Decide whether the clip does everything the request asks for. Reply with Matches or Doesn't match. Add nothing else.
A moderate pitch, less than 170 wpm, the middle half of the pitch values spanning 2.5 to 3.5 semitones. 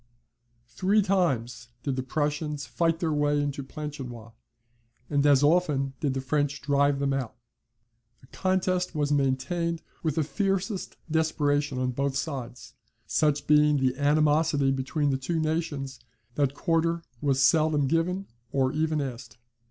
Matches